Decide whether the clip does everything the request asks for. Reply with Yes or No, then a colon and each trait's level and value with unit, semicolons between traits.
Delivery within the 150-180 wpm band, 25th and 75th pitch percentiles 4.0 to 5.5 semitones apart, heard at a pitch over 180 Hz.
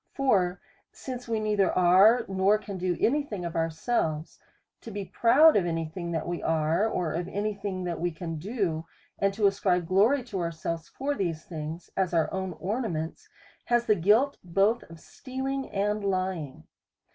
Yes: average, 175 wpm; average, 4.3 semitones; high, 190 Hz